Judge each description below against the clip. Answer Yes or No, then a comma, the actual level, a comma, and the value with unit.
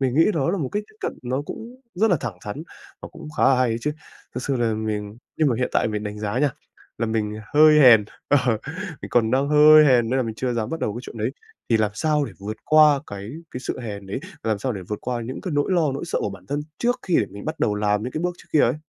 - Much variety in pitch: Yes, wide, 5.9 semitones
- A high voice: No, low, 125 Hz